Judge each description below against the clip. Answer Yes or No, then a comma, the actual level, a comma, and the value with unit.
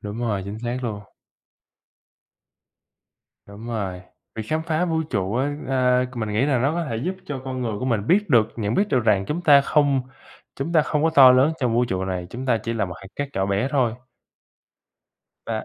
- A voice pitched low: Yes, low, 125 Hz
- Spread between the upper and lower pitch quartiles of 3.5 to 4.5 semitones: No, average, 5.0 semitones